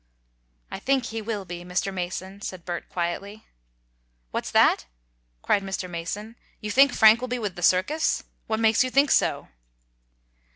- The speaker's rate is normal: Yes, average, 160 wpm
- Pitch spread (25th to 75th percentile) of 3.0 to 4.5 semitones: Yes, average, 3.9 semitones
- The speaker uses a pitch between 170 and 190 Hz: No, high, 205 Hz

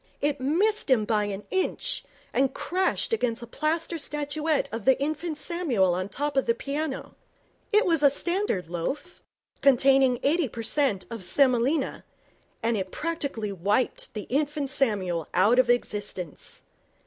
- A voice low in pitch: No, very high, 270 Hz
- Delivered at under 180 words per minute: Yes, average, 150 wpm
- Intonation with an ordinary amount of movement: No, wide, 6.0 semitones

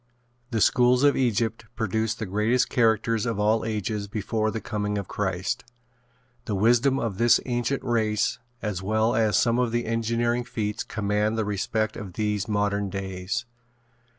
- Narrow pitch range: Yes, narrow, 2.2 semitones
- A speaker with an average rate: Yes, average, 155 wpm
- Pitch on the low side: Yes, low, 110 Hz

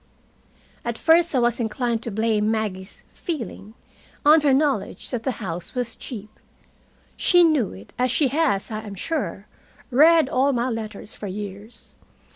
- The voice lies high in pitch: Yes, high, 235 Hz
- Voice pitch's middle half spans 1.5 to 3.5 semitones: No, average, 4.8 semitones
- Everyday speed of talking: Yes, average, 155 wpm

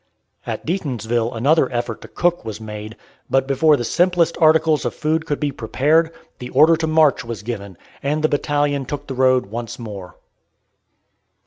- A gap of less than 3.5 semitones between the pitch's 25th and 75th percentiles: No, average, 5.1 semitones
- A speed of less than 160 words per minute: No, average, 165 wpm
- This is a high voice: No, low, 135 Hz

